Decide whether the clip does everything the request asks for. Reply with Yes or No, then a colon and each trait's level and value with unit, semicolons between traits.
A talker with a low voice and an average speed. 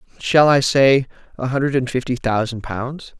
Yes: low, 130 Hz; average, 170 wpm